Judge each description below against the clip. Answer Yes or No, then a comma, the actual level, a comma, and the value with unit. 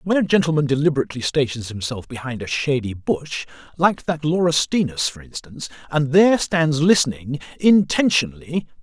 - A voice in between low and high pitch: Yes, medium, 145 Hz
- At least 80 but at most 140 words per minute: Yes, slow, 135 wpm